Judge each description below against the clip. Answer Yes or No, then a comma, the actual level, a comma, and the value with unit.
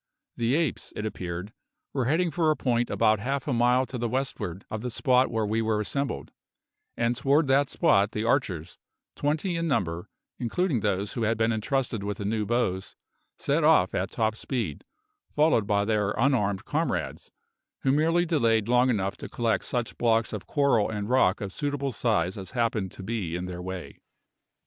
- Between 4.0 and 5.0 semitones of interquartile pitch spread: Yes, average, 4.5 semitones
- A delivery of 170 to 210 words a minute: Yes, average, 180 wpm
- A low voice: Yes, low, 115 Hz